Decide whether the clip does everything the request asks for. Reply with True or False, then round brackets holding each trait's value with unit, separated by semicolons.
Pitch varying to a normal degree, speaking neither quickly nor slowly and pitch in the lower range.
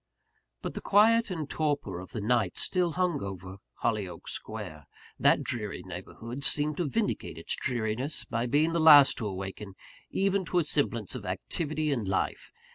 False (7.5 semitones; 165 wpm; 130 Hz)